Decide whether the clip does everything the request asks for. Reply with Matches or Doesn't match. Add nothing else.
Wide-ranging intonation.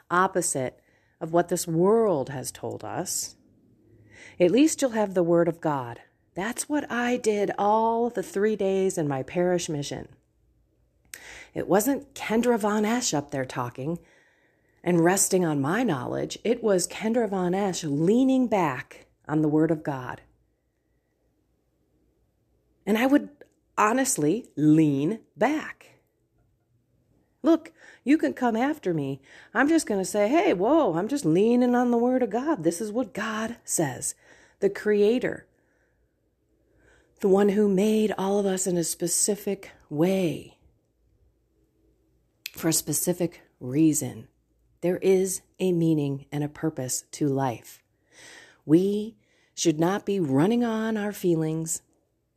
Matches